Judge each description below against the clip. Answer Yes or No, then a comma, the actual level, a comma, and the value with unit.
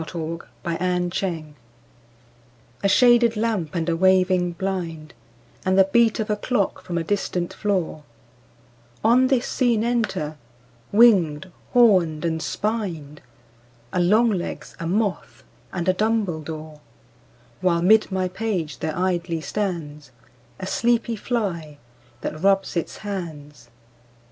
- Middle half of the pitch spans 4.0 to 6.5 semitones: Yes, average, 4.6 semitones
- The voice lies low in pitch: No, medium, 185 Hz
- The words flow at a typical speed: No, slow, 120 wpm